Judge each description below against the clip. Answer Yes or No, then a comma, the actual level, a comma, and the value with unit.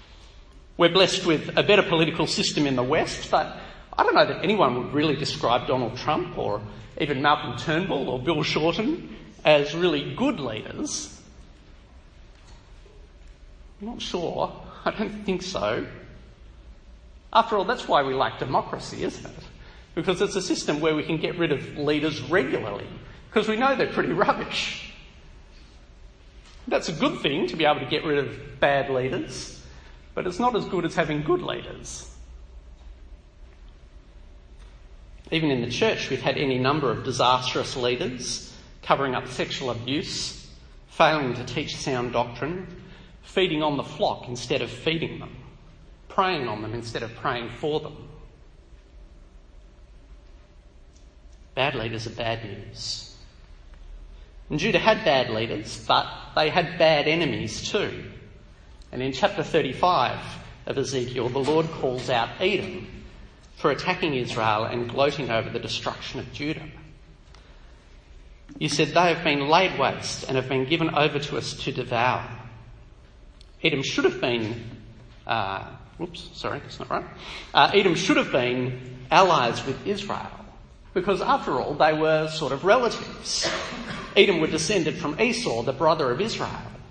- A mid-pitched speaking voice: No, low, 125 Hz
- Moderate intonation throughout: No, wide, 8.5 semitones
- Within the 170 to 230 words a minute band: No, average, 145 wpm